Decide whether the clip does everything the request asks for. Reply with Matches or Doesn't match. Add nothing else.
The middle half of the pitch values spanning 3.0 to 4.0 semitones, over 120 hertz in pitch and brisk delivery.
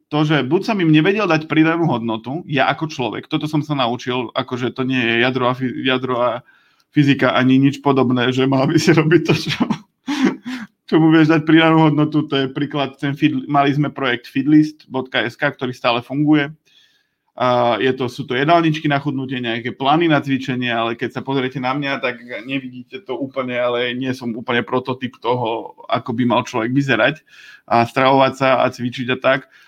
Matches